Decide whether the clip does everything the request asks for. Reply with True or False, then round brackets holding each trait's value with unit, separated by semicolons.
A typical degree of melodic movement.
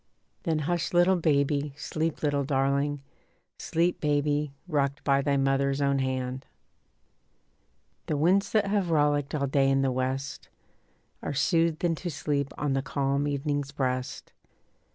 False (2.2 semitones)